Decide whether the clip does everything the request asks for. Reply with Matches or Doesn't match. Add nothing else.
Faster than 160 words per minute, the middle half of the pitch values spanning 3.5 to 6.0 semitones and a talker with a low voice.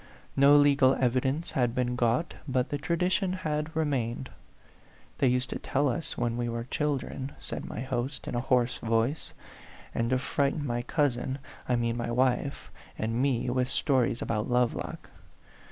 Doesn't match